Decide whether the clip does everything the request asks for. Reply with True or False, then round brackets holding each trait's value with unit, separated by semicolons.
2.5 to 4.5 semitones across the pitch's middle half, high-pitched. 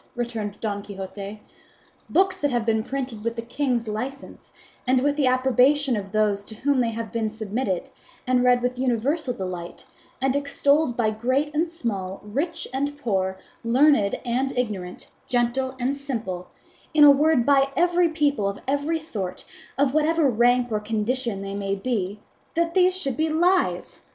False (4.9 semitones; 245 Hz)